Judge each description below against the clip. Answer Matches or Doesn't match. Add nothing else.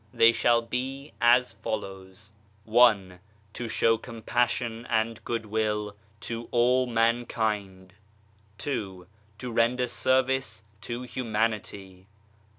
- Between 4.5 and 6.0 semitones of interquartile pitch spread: Doesn't match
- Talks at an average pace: Doesn't match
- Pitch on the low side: Matches